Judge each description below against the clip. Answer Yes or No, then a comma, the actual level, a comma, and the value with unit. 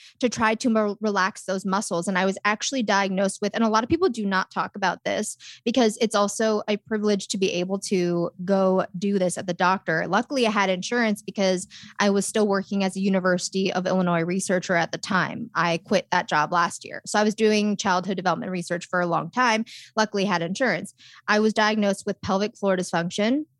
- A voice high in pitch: Yes, high, 195 Hz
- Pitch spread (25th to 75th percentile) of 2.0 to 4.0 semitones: Yes, average, 2.7 semitones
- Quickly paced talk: Yes, fast, 210 wpm